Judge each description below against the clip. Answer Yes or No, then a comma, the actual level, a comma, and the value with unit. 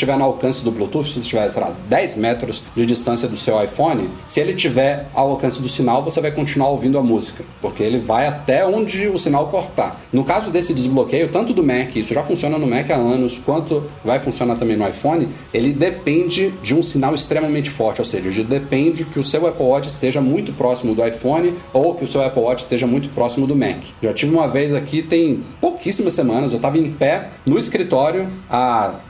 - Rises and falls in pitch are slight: No, average, 4.1 semitones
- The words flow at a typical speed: No, fast, 215 wpm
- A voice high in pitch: No, medium, 140 Hz